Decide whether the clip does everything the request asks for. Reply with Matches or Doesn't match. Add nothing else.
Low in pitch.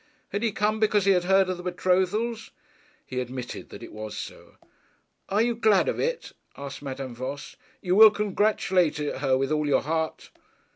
Doesn't match